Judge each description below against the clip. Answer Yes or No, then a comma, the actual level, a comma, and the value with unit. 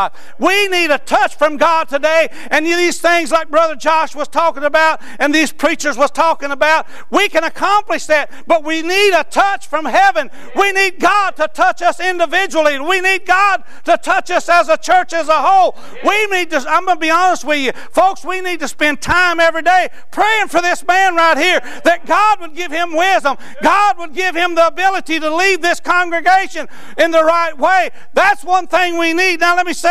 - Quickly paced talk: Yes, fast, 210 wpm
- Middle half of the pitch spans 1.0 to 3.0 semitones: Yes, average, 2.7 semitones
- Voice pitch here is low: No, very high, 335 Hz